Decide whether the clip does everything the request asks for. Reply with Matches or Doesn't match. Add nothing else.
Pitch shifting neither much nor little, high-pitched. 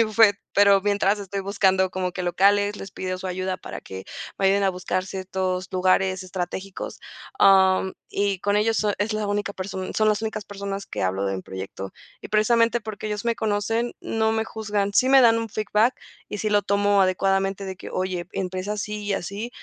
Doesn't match